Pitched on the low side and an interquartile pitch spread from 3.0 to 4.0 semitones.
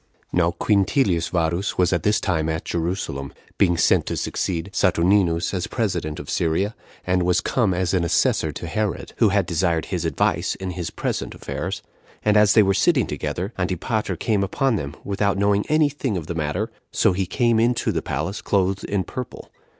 Yes: very low, 95 Hz; average, 3.5 semitones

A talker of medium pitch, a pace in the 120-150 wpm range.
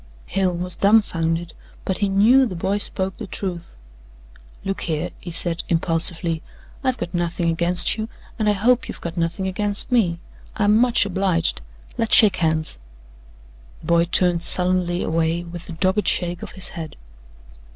No: medium, 180 Hz; average, 160 wpm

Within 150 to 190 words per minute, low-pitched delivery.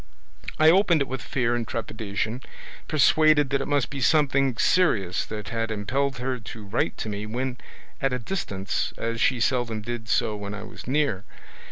Yes: average, 180 wpm; low, 120 Hz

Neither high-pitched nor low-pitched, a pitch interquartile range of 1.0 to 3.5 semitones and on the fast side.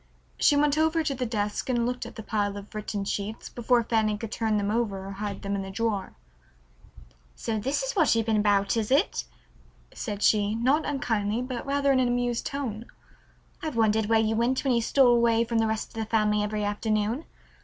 No: high, 225 Hz; average, 3.0 semitones; fast, 210 wpm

